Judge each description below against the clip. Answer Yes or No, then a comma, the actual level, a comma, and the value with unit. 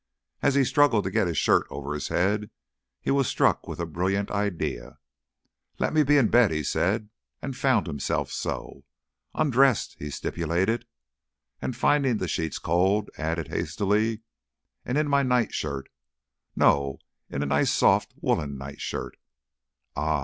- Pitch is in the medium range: No, low, 100 Hz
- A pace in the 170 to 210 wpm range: No, average, 150 wpm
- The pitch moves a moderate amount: No, wide, 8.1 semitones